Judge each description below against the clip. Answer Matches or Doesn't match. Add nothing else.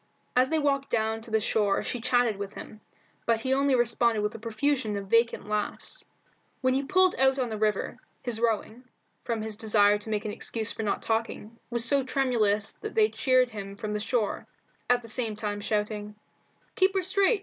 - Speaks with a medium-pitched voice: Doesn't match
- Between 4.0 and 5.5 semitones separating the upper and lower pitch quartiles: Doesn't match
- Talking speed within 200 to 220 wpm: Matches